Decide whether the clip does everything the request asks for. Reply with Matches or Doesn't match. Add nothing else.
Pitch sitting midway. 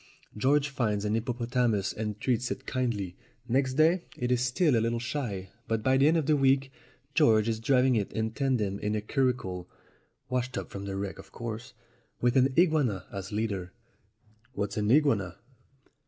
Doesn't match